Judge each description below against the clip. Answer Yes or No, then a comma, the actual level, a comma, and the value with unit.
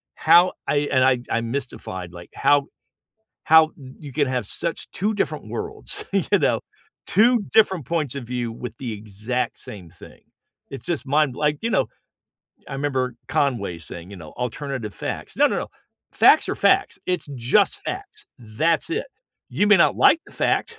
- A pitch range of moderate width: No, wide, 6.0 semitones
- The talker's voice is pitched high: No, low, 135 Hz